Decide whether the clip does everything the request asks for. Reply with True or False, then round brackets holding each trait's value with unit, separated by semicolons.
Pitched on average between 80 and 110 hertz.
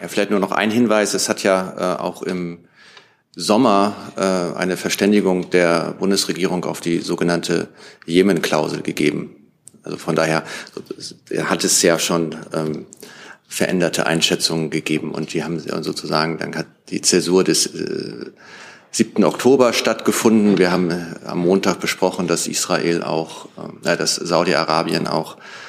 True (85 Hz)